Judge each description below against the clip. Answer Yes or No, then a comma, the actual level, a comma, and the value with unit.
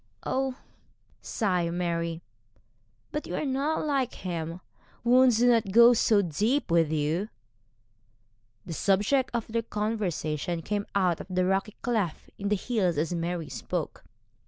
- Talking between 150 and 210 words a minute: No, average, 140 wpm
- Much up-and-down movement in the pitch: Yes, wide, 5.7 semitones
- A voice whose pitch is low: No, high, 195 Hz